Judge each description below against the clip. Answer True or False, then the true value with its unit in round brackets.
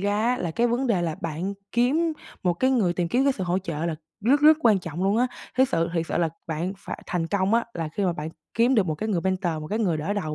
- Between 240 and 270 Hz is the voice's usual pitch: False (190 Hz)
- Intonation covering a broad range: True (5.7 semitones)